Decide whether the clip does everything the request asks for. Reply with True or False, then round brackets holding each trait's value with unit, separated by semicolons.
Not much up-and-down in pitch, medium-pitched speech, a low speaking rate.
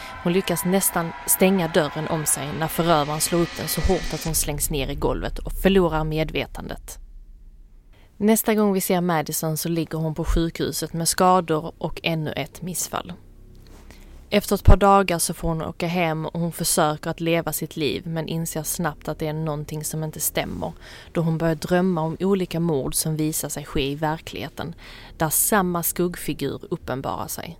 False (2.3 semitones; 160 Hz; 180 wpm)